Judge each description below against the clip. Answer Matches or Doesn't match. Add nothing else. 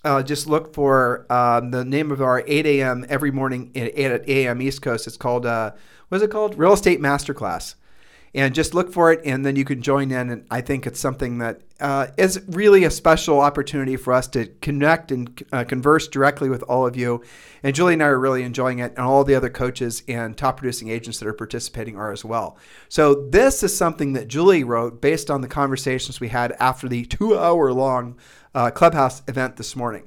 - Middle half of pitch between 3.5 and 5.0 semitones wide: Doesn't match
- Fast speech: Matches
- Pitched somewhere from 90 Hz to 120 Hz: Doesn't match